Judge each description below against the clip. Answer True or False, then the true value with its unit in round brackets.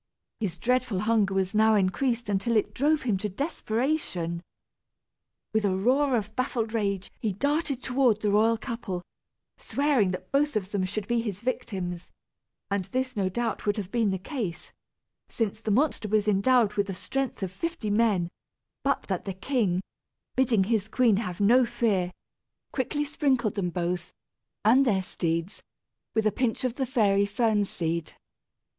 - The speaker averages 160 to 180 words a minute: True (165 wpm)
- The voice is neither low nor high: False (215 Hz)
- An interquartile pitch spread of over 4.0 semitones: True (4.6 semitones)